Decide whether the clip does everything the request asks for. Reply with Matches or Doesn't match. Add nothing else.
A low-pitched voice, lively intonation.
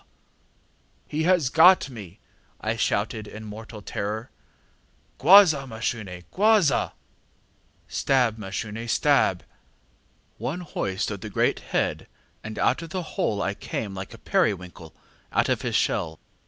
Matches